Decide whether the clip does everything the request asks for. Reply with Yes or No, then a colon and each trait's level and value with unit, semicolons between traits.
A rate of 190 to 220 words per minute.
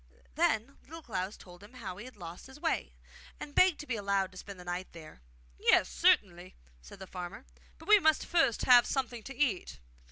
Yes: average, 200 wpm